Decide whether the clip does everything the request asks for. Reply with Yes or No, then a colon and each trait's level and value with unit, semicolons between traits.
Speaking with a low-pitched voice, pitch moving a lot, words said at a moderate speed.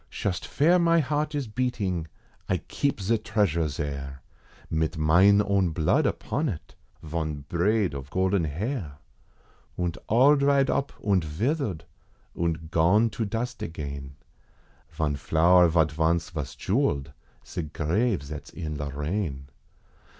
No: very low, 85 Hz; wide, 6.3 semitones; slow, 130 wpm